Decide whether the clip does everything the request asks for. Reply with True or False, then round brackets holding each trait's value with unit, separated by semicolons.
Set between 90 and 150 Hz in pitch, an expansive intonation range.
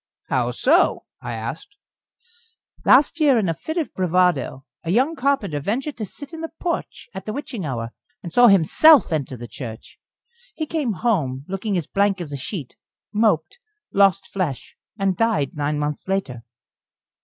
False (195 Hz; 8.7 semitones)